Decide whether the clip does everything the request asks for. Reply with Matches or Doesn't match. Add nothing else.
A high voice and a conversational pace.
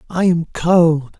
Doesn't match